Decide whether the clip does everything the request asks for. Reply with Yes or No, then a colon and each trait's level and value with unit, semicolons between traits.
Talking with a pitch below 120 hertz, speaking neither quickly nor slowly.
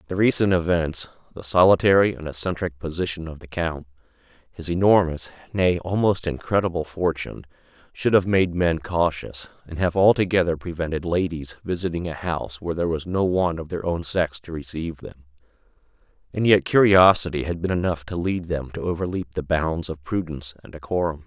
Yes: very low, 85 Hz; average, 165 wpm